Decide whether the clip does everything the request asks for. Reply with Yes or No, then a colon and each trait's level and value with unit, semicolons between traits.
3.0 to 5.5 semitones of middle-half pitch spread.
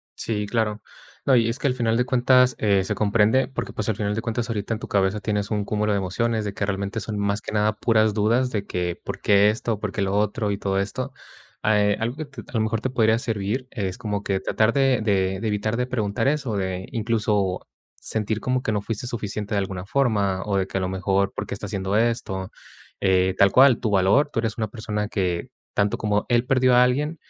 No: narrow, 2.6 semitones